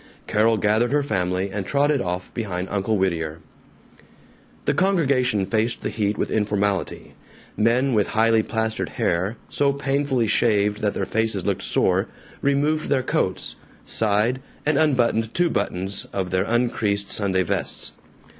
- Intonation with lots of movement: No, average, 4.3 semitones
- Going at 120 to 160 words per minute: Yes, average, 140 wpm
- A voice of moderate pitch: No, low, 110 Hz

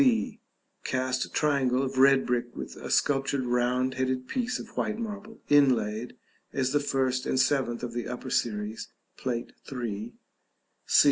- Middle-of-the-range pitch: No, low, 130 Hz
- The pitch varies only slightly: Yes, narrow, 2.3 semitones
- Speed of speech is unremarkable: Yes, average, 150 wpm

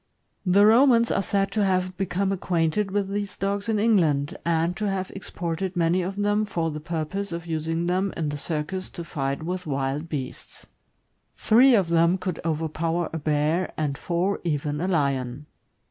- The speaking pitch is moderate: Yes, medium, 175 Hz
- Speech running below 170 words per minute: No, average, 175 wpm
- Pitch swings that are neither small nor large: Yes, average, 3.8 semitones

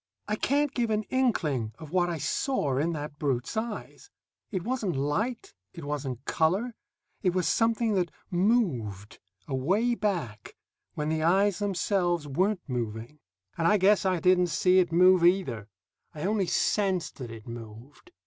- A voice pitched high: No, medium, 175 Hz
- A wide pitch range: Yes, wide, 6.4 semitones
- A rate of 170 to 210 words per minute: No, average, 155 wpm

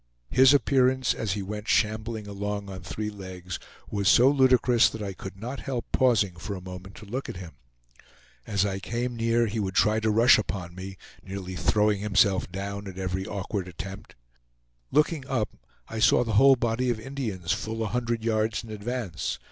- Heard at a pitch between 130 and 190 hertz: No, low, 105 Hz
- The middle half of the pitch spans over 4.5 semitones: No, average, 3.4 semitones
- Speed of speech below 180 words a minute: No, average, 185 wpm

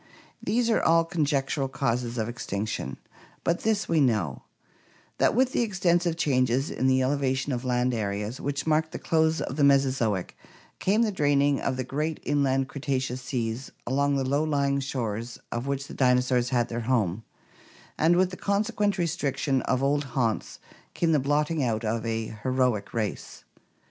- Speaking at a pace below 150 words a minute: No, average, 165 wpm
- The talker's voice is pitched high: No, low, 135 Hz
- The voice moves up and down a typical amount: Yes, average, 4.1 semitones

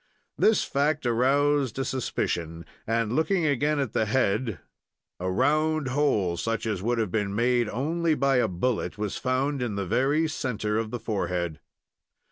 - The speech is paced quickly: No, average, 160 wpm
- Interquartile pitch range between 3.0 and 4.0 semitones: No, average, 5.2 semitones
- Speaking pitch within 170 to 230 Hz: No, low, 125 Hz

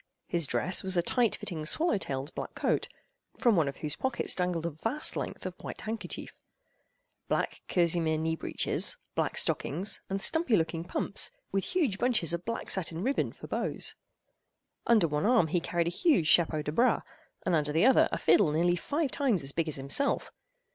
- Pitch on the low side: No, medium, 175 Hz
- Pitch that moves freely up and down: Yes, wide, 6.2 semitones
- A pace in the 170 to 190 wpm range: Yes, average, 185 wpm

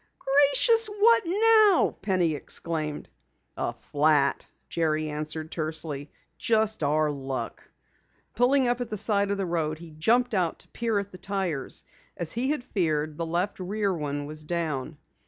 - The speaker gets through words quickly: No, average, 155 wpm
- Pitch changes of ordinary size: No, wide, 6.8 semitones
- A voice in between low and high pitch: Yes, medium, 170 Hz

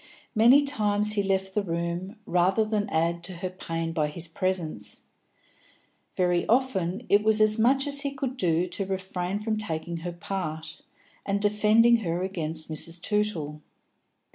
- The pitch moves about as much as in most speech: Yes, average, 4.0 semitones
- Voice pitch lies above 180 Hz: Yes, high, 190 Hz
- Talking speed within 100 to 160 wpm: Yes, average, 155 wpm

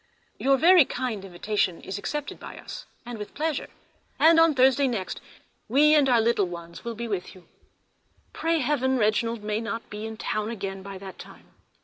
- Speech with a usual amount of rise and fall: Yes, average, 4.8 semitones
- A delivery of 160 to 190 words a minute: Yes, average, 170 wpm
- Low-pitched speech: No, high, 230 Hz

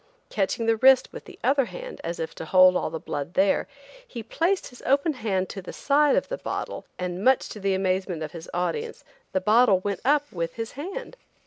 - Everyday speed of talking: No, fast, 215 wpm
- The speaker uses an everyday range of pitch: No, wide, 7.3 semitones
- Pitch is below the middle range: No, high, 220 Hz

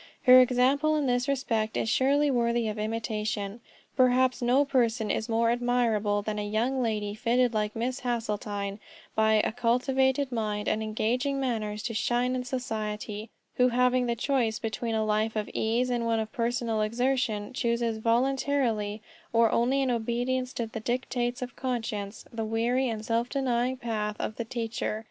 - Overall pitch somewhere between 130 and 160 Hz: No, high, 235 Hz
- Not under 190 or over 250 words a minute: No, average, 165 wpm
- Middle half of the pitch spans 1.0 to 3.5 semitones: Yes, narrow, 2.5 semitones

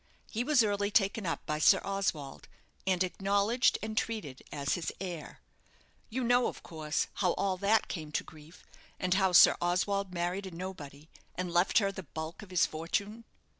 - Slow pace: No, average, 175 wpm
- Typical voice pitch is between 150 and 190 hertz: Yes, medium, 185 Hz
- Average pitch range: Yes, average, 3.5 semitones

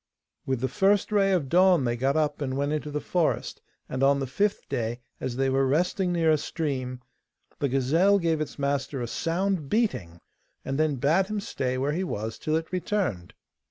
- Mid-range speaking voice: Yes, medium, 150 Hz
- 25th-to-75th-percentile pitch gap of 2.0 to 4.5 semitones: No, average, 5.3 semitones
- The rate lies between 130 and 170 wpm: No, average, 195 wpm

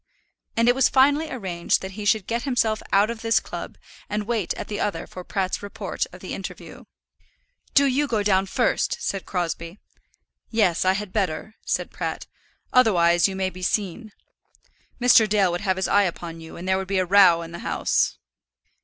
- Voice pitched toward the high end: Yes, high, 200 Hz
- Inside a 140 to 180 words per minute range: No, average, 190 wpm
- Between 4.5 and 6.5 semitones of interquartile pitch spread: No, average, 3.5 semitones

